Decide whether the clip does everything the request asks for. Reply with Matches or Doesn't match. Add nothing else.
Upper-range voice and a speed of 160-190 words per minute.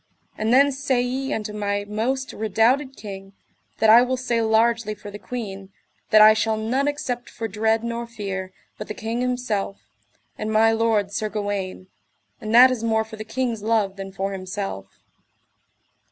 Matches